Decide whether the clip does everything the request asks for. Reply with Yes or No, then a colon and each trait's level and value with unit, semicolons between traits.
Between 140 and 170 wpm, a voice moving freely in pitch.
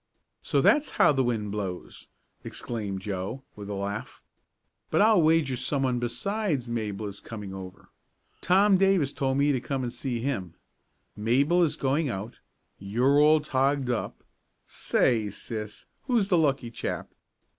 Yes: average, 145 wpm; wide, 5.7 semitones